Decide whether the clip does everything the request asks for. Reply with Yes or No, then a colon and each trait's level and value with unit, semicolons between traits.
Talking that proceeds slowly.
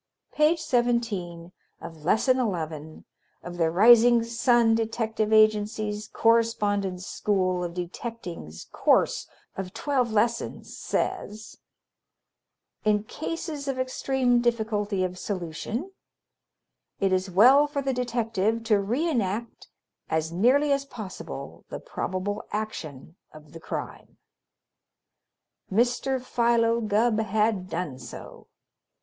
Yes: slow, 105 wpm